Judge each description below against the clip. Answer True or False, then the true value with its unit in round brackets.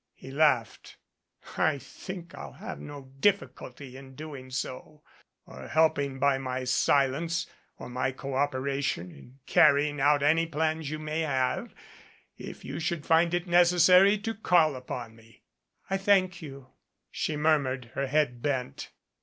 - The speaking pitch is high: False (145 Hz)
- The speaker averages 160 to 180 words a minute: False (140 wpm)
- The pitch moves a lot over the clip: False (3.6 semitones)